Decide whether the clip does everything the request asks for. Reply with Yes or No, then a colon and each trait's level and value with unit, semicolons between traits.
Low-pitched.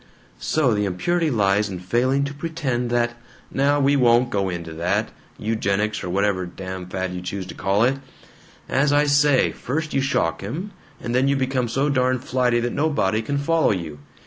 Yes: low, 120 Hz